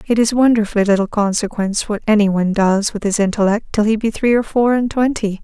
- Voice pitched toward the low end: No, high, 215 Hz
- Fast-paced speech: Yes, fast, 220 wpm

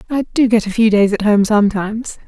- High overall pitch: Yes, high, 215 Hz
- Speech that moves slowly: No, fast, 235 wpm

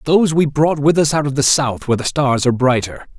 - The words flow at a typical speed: No, fast, 265 wpm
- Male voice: Yes, male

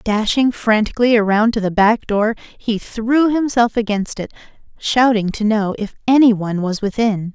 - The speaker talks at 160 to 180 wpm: Yes, average, 165 wpm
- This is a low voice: No, high, 220 Hz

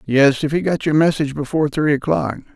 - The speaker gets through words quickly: Yes, fast, 210 wpm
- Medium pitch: Yes, medium, 145 Hz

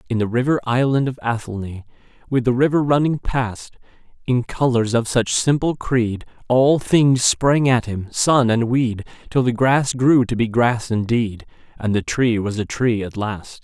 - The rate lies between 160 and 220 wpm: Yes, average, 180 wpm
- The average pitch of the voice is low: Yes, low, 120 Hz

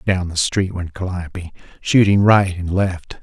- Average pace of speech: Yes, average, 170 wpm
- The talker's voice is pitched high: No, very low, 90 Hz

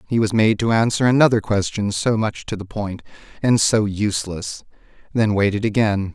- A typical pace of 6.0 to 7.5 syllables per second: No, 5.1 syllables/s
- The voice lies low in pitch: Yes, low, 105 Hz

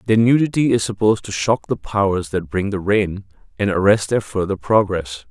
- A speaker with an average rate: Yes, average, 190 wpm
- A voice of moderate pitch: No, low, 100 Hz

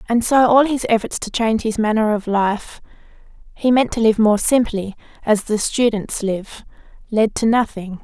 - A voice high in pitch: Yes, high, 220 Hz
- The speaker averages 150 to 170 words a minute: No, average, 180 wpm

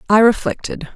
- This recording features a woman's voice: Yes, female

